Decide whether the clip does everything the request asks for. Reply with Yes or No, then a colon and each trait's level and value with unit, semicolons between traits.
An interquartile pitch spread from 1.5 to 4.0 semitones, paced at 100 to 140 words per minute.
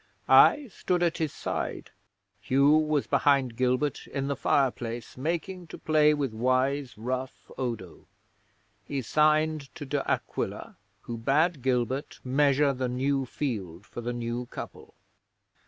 Yes: average, 3.3 semitones; slow, 135 wpm